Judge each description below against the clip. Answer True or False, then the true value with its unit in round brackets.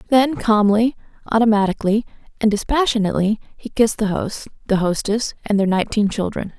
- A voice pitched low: False (215 Hz)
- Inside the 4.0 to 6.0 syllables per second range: True (5.9 syllables/s)